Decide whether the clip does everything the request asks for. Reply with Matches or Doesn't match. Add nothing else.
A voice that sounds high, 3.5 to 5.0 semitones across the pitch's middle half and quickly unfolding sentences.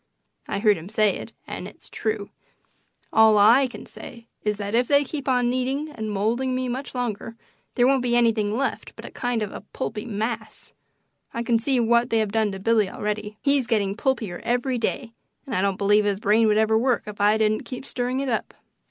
Doesn't match